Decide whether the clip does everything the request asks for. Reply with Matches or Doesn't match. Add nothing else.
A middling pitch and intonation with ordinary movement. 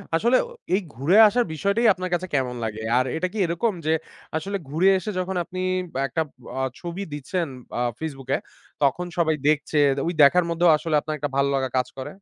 Matches